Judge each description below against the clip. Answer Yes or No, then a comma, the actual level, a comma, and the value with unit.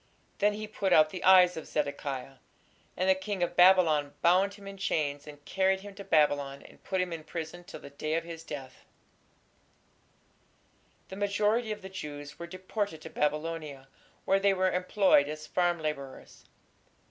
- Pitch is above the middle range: No, medium, 175 Hz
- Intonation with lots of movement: No, average, 4.3 semitones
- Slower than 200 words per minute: Yes, average, 170 wpm